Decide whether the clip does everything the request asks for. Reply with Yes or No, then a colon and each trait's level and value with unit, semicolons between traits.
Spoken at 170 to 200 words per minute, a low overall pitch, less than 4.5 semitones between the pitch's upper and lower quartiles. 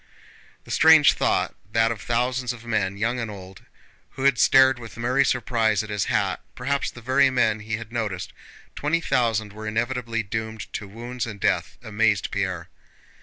Yes: average, 175 wpm; low, 115 Hz; average, 2.8 semitones